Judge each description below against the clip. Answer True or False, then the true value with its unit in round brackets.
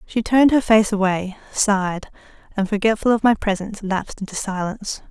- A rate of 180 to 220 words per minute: False (165 wpm)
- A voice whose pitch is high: True (205 Hz)